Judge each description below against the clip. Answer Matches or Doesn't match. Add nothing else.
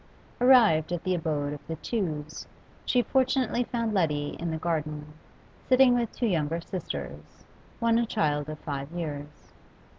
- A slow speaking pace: Doesn't match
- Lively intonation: Matches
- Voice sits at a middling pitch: Matches